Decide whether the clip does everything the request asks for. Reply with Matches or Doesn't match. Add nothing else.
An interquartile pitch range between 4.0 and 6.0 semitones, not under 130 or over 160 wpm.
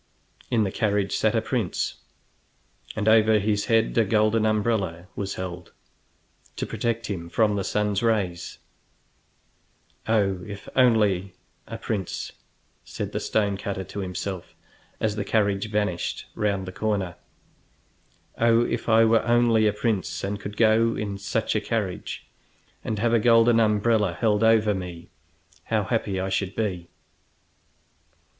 Doesn't match